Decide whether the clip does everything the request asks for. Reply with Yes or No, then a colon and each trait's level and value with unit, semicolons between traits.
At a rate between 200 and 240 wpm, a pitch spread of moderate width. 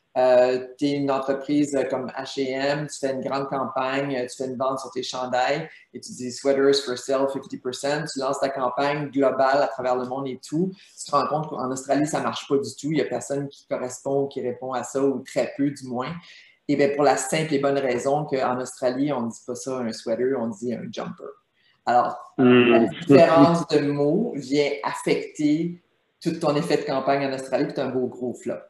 No: average, 215 wpm; narrow, 2.1 semitones